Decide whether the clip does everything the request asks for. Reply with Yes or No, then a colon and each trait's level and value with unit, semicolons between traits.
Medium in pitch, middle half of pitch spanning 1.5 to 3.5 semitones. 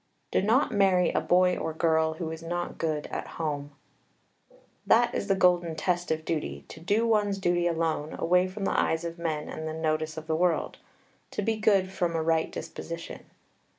Yes: medium, 170 Hz; average, 2.7 semitones